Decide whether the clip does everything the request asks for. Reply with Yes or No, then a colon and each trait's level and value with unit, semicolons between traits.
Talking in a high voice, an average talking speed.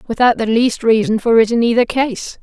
No: high, 230 Hz; fast, 220 wpm